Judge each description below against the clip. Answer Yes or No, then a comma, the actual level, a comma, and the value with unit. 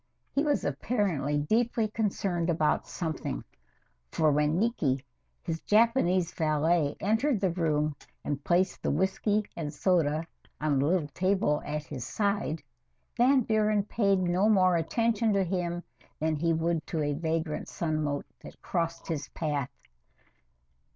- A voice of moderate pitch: Yes, medium, 170 Hz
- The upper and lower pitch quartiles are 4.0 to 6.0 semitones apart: Yes, average, 4.9 semitones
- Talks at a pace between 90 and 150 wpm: Yes, slow, 135 wpm